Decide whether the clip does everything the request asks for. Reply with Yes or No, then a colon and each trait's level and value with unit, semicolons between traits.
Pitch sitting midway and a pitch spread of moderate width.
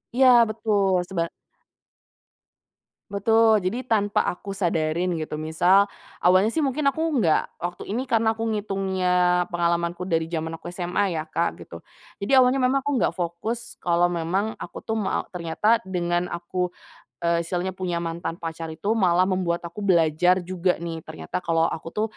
Yes: medium, 180 Hz; average, 3.8 semitones